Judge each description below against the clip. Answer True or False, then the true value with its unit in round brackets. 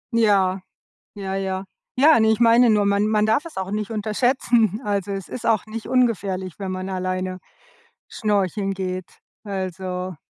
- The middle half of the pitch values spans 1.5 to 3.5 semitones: True (2.8 semitones)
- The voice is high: True (200 Hz)